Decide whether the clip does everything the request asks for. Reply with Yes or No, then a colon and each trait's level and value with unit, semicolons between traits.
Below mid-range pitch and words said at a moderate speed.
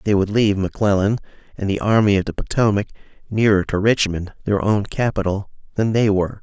Yes: low, 100 Hz; average, 175 wpm